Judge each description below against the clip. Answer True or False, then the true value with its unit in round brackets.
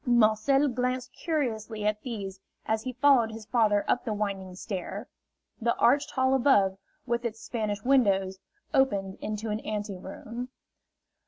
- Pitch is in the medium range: False (220 Hz)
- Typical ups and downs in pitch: True (3.5 semitones)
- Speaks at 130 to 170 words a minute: True (140 wpm)